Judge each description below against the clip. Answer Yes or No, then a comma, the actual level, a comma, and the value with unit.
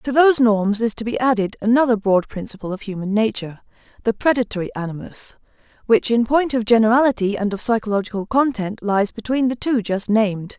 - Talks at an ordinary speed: Yes, average, 165 wpm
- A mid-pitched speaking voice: No, high, 220 Hz